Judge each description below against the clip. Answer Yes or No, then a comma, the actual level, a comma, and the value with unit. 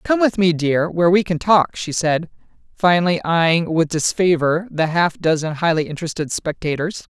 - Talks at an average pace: Yes, average, 170 wpm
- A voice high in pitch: No, medium, 170 Hz